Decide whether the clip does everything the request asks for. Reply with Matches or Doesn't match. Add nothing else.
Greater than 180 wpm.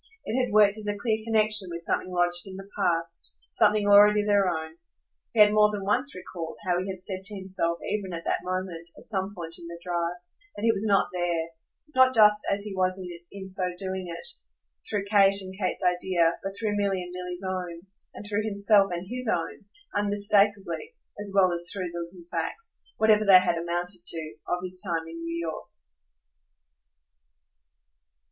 Matches